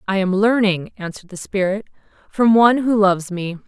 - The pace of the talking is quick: No, average, 180 wpm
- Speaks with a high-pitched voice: Yes, high, 200 Hz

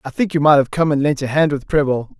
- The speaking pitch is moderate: Yes, medium, 145 Hz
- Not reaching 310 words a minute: No, fast, 330 wpm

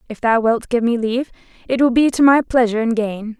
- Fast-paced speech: Yes, fast, 245 wpm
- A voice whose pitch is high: Yes, high, 240 Hz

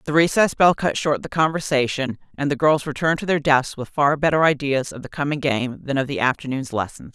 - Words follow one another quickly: Yes, fast, 225 wpm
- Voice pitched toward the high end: No, medium, 145 Hz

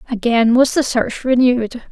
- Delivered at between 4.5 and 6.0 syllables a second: Yes, 5.0 syllables/s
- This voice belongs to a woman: Yes, female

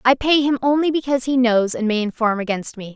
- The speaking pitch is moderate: No, high, 245 Hz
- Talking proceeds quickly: Yes, fast, 245 wpm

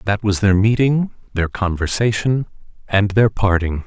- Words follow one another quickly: No, average, 140 wpm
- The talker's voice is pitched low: Yes, low, 105 Hz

